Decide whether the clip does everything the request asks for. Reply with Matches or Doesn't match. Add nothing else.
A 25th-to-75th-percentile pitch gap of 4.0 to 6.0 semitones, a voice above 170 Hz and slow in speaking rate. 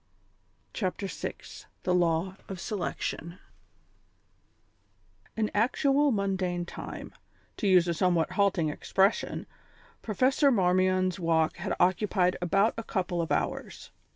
Doesn't match